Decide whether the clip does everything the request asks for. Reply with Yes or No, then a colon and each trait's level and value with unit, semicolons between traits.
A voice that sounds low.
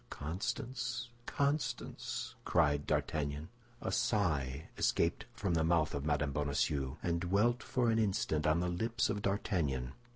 Yes: very low, 85 Hz